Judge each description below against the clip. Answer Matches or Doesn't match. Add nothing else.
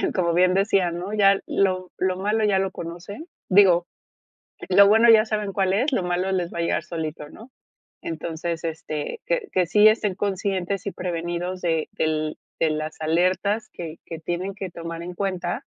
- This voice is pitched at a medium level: Matches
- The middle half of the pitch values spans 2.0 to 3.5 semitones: Matches